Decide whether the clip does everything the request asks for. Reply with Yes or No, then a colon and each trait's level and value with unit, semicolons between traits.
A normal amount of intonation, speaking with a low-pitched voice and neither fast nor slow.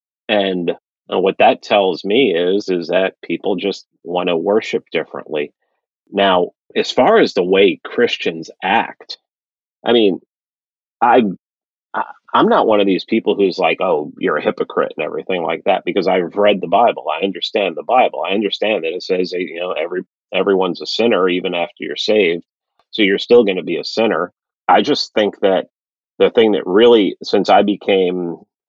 Yes: average, 3.3 semitones; very low, 95 Hz; average, 180 wpm